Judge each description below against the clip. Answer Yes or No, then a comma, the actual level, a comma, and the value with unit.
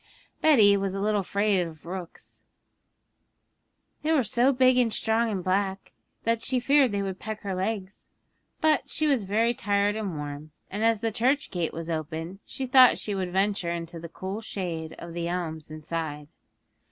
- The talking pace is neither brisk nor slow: Yes, average, 175 wpm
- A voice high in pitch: Yes, high, 195 Hz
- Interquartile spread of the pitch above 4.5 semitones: Yes, average, 4.9 semitones